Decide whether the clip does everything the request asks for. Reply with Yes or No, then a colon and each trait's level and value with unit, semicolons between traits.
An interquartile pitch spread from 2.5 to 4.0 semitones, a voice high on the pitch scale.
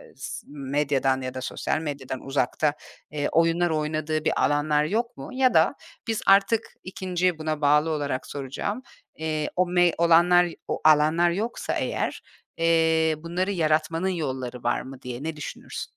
No: average, 3.3 semitones; medium, 155 Hz